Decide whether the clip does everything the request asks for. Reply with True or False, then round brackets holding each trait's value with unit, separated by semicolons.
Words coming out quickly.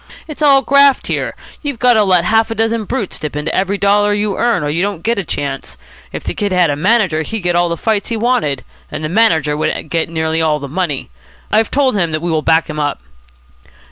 True (235 wpm)